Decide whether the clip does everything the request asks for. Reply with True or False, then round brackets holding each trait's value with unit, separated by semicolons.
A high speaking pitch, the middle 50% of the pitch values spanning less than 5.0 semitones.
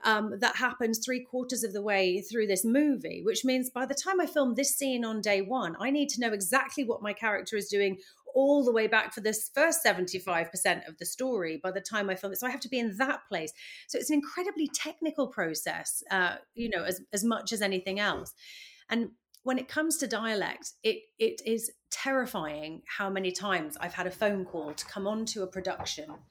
False (225 Hz; 5.3 semitones)